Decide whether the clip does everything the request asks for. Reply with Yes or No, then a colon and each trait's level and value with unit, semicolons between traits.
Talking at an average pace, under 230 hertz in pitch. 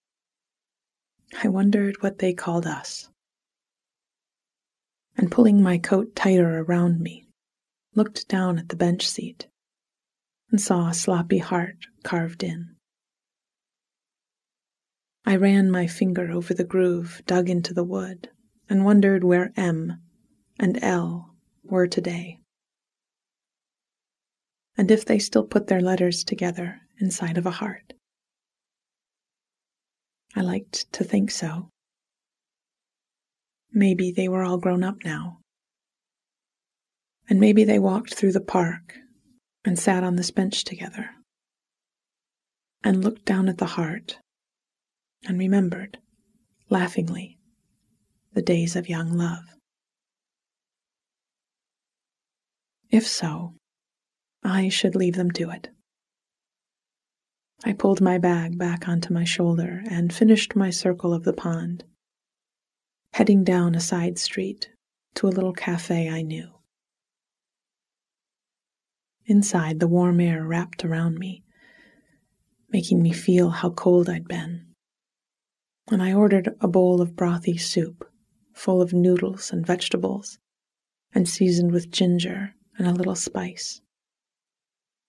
No: slow, 115 wpm; medium, 185 Hz